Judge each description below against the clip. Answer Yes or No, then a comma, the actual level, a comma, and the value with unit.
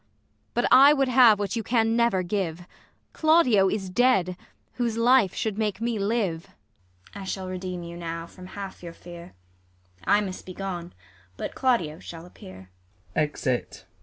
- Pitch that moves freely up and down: No, average, 4.9 semitones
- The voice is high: Yes, high, 195 Hz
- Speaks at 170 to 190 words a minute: No, average, 155 wpm